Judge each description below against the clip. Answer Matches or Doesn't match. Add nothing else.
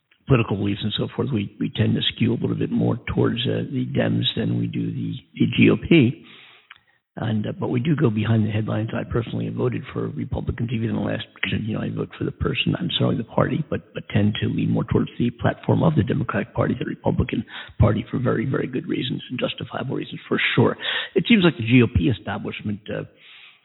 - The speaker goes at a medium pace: Doesn't match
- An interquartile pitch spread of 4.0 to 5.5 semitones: Doesn't match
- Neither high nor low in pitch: Doesn't match